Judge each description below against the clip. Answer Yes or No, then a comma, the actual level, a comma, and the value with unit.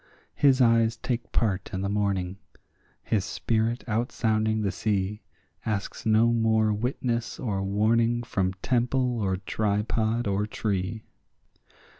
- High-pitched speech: No, low, 110 Hz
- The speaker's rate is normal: No, slow, 125 wpm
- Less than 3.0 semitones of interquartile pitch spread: Yes, narrow, 2.6 semitones